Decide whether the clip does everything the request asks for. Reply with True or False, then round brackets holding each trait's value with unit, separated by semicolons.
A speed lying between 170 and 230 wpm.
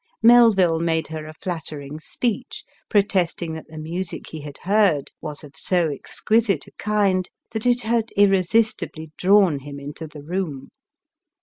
False (150 wpm)